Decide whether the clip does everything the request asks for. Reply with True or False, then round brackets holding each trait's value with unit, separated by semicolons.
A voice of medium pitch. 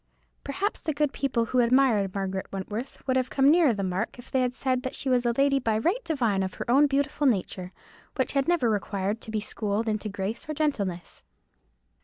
False (245 Hz)